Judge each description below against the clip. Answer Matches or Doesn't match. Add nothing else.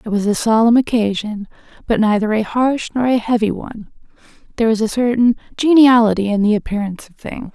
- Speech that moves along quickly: Doesn't match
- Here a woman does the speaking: Matches